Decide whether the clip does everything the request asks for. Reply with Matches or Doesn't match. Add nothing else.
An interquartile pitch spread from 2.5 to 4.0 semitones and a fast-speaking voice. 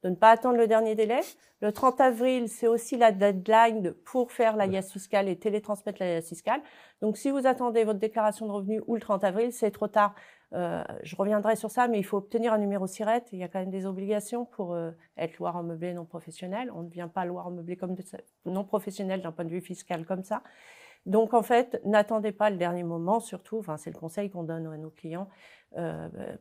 Matches